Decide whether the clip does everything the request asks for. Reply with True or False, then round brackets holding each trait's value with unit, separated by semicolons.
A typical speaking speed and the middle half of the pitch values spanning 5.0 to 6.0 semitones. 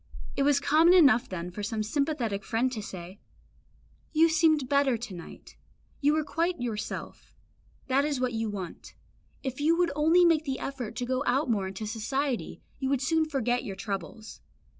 True (180 wpm; 5.6 semitones)